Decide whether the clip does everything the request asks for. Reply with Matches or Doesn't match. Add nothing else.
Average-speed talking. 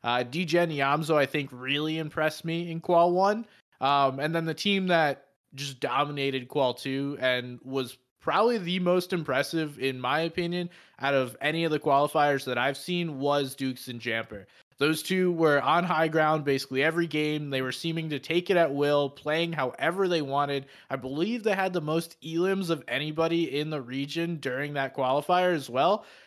Matches